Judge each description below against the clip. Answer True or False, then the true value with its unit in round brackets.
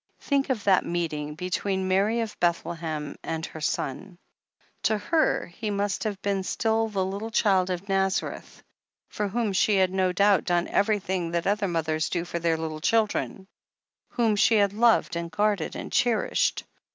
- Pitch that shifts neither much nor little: True (3.5 semitones)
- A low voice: False (190 Hz)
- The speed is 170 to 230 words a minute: True (175 wpm)